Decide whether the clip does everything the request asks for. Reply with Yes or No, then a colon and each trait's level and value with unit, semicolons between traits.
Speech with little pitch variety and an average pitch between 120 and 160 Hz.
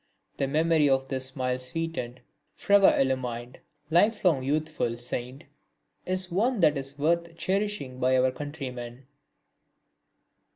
No: average, 4.6 semitones; medium, 140 Hz